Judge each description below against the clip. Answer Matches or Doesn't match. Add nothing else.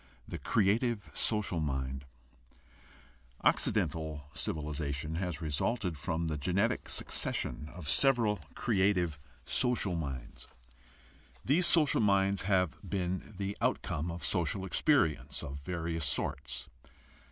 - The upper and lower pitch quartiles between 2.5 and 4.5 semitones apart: Doesn't match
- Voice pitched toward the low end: Matches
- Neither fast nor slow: Doesn't match